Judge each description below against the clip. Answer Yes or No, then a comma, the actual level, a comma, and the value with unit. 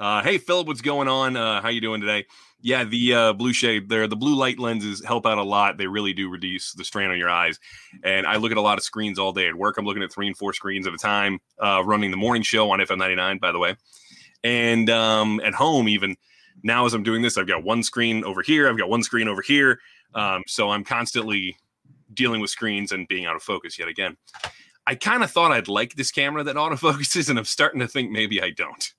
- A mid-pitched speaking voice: No, low, 110 Hz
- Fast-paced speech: Yes, fast, 250 wpm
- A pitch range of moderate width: Yes, average, 3.2 semitones